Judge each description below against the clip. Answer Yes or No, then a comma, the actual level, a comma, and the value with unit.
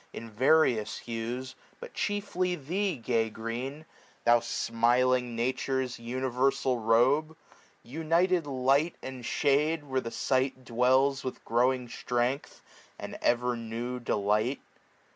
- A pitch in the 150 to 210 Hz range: No, low, 130 Hz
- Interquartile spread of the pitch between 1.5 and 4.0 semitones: Yes, average, 3.0 semitones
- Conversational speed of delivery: No, slow, 115 wpm